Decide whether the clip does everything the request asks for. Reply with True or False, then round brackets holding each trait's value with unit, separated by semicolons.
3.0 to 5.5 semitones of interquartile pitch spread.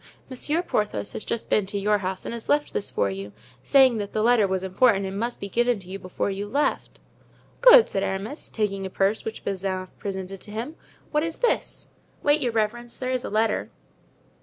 True (4.1 semitones)